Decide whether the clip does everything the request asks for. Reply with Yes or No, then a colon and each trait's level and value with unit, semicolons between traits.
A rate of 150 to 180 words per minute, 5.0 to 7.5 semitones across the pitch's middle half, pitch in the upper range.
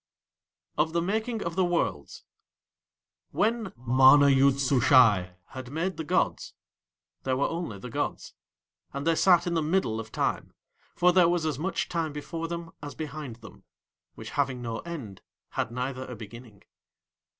No: average, 160 wpm; average, 5.3 semitones; medium, 145 Hz